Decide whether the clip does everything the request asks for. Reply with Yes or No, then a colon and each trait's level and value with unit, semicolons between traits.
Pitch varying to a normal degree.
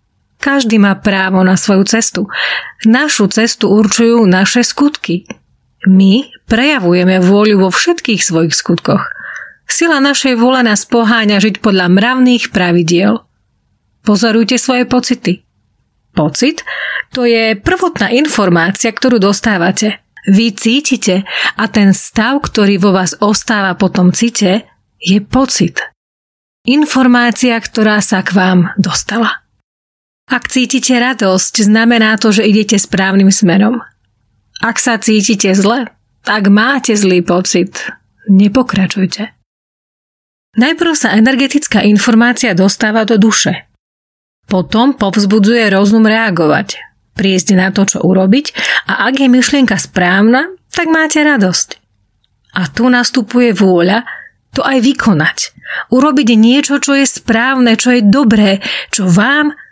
Yes: average, 4.4 semitones